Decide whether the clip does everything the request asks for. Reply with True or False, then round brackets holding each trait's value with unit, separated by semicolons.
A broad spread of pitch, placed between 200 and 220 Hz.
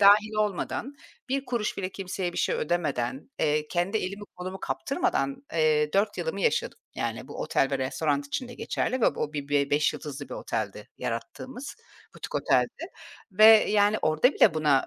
False (6.3 semitones; 185 Hz)